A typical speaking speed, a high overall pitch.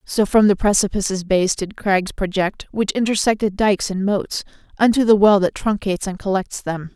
Yes: average, 180 wpm; high, 200 Hz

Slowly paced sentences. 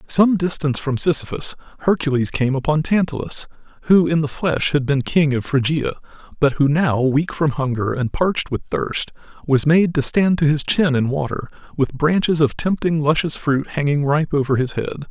No: average, 185 wpm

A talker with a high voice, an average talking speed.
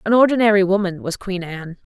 Yes: high, 195 Hz; average, 190 wpm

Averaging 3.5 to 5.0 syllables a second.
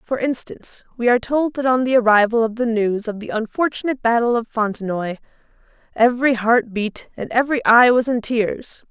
No: 5.5 syllables/s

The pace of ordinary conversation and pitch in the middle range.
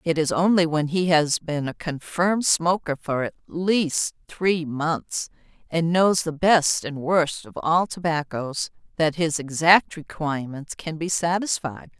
Yes: average, 155 wpm; medium, 160 Hz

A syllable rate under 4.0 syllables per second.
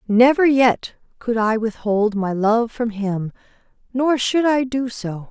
Yes: 3.7 syllables/s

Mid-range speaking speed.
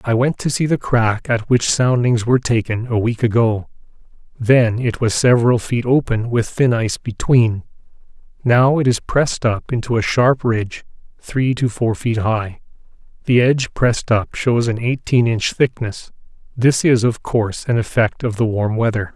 Yes: average, 170 wpm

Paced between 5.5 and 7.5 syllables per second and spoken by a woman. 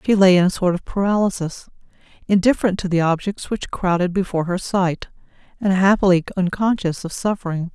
Yes: 5.8 syllables/s; female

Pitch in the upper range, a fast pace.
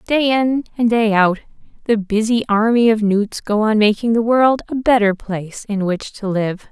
No: high, 220 Hz; average, 195 wpm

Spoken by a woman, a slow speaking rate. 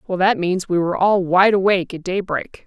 No: female; fast, 225 wpm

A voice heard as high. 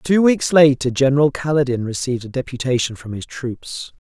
No: low, 135 Hz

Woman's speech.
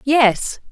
Yes: female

